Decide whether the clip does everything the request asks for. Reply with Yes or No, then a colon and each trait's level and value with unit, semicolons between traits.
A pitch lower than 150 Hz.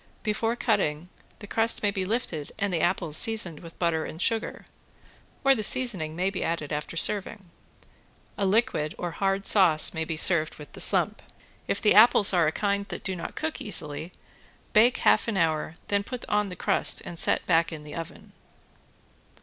No: medium, 185 Hz